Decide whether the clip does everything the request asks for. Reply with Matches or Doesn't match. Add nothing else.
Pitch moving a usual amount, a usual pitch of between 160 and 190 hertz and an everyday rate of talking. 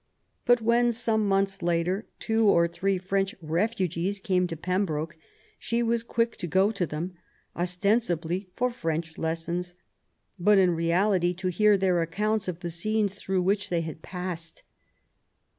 Matches